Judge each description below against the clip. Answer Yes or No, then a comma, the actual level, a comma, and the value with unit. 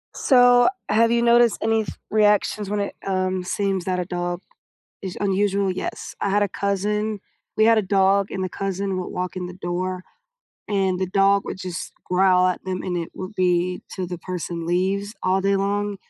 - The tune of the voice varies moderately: No, narrow, 1.9 semitones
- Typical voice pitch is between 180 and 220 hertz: Yes, high, 190 Hz